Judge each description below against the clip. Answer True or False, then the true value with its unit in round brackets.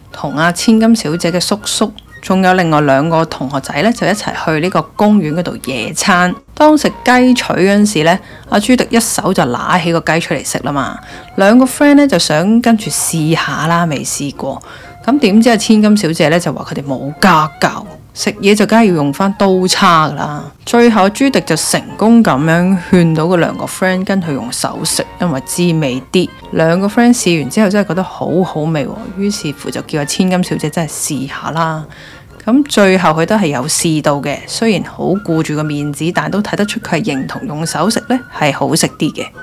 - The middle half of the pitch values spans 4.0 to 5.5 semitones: True (5.1 semitones)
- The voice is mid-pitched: True (180 Hz)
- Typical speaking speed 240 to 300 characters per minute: False (310 characters per minute)